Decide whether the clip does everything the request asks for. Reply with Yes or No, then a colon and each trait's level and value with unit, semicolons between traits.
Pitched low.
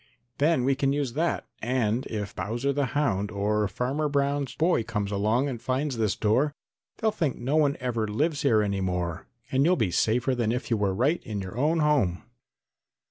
Yes: low, 125 Hz